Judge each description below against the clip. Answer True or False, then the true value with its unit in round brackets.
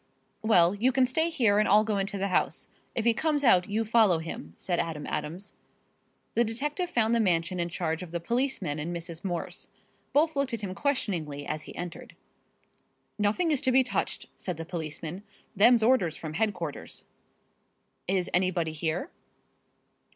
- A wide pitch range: True (5.9 semitones)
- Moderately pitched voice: False (195 Hz)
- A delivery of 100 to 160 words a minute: False (170 wpm)